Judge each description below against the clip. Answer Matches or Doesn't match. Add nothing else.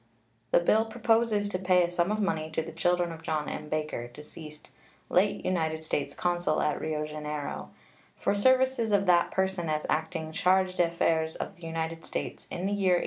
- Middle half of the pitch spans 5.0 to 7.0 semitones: Doesn't match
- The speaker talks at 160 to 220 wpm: Matches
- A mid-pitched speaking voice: Matches